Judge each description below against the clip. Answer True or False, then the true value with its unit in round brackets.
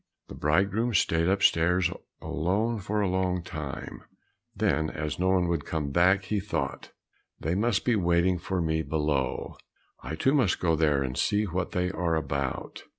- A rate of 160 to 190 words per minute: True (165 wpm)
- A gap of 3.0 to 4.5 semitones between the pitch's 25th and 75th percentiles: True (3.5 semitones)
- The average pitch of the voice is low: True (90 Hz)